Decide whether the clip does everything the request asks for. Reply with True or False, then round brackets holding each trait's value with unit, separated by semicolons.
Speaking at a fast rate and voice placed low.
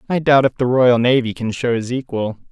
True (240 wpm; 125 Hz)